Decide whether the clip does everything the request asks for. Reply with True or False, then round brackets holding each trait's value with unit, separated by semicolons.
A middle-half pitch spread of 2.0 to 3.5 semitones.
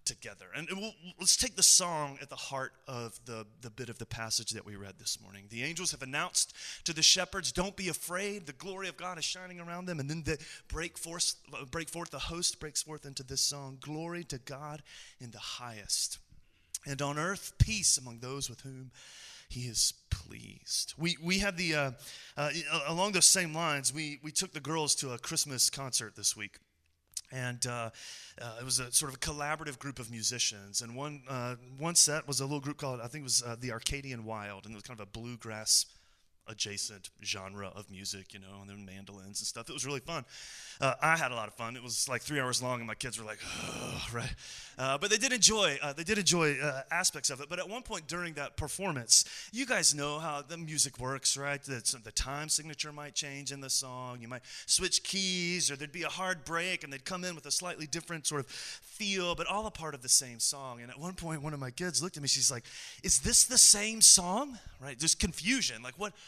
False (5.6 semitones)